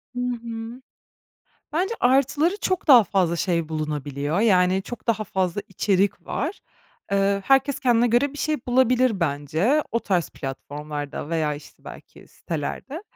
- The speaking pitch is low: No, high, 205 Hz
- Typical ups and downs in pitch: No, wide, 7.6 semitones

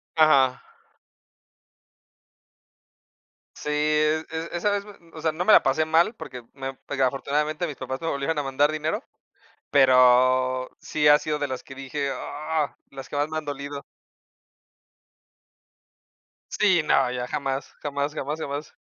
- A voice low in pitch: No, medium, 145 Hz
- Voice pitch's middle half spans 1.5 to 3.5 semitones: Yes, narrow, 2.6 semitones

